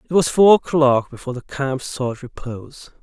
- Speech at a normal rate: Yes, average, 180 wpm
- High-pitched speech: No, medium, 140 Hz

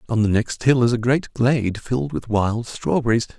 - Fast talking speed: Yes, fast, 215 wpm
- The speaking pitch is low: Yes, low, 115 Hz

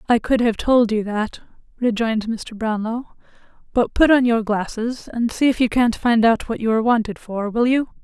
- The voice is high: Yes, high, 230 Hz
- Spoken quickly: Yes, fast, 210 wpm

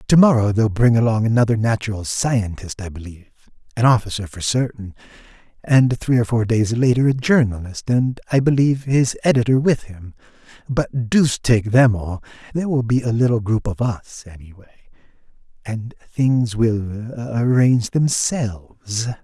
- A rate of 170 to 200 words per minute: No, average, 150 wpm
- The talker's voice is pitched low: Yes, low, 115 Hz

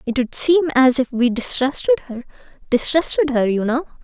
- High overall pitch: Yes, very high, 265 Hz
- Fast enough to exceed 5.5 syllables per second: No, 5.0 syllables/s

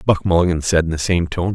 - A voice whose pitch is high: No, very low, 85 Hz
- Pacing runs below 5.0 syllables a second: No, 6.3 syllables/s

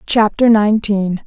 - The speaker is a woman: Yes, female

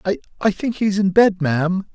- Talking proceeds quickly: No, average, 185 wpm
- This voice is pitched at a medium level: No, high, 195 Hz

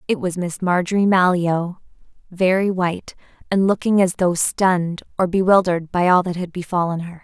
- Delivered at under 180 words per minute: Yes, average, 165 wpm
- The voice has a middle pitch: Yes, medium, 180 Hz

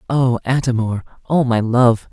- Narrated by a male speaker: Yes, male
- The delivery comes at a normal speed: Yes, average, 170 wpm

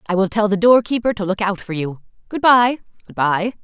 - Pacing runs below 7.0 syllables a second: Yes, 5.5 syllables/s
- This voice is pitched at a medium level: No, high, 205 Hz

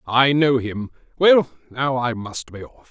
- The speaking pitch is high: No, low, 130 Hz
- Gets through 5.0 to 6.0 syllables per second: No, 4.4 syllables/s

